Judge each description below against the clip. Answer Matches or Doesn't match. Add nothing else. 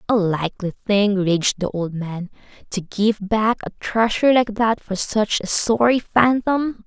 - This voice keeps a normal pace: Matches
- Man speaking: Doesn't match